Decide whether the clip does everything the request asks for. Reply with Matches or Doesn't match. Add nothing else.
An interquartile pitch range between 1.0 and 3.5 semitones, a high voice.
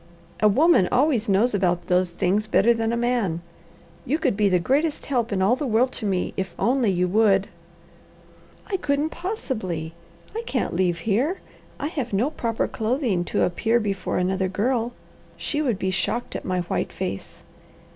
Doesn't match